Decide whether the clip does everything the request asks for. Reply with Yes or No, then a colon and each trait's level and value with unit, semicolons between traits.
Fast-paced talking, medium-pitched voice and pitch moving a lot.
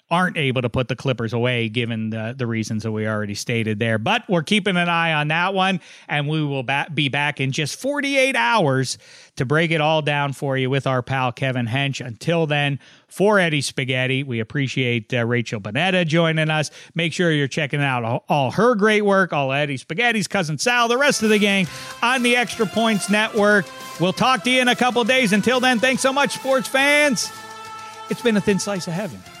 Yes: fast, 215 wpm; medium, 160 Hz; wide, 8.5 semitones